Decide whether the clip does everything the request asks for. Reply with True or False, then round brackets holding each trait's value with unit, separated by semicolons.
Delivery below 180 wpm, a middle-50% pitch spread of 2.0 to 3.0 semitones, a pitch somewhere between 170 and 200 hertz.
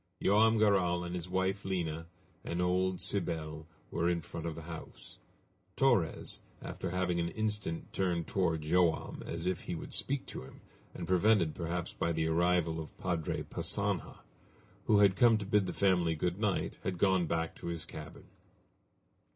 False (170 wpm; 2.6 semitones; 90 Hz)